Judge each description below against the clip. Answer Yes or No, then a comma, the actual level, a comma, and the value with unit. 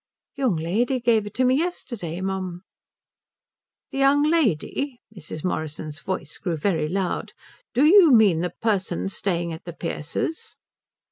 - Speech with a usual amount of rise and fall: No, wide, 7.3 semitones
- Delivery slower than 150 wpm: Yes, average, 140 wpm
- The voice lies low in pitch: No, high, 195 Hz